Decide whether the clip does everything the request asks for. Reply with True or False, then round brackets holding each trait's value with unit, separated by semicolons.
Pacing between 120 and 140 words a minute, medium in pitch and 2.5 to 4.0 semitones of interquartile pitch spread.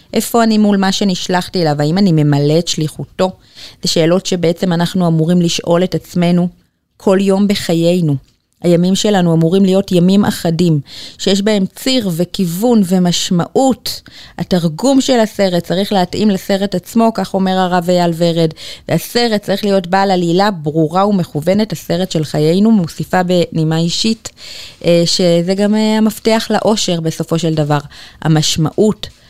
True (135 wpm; 180 Hz; 3.2 semitones)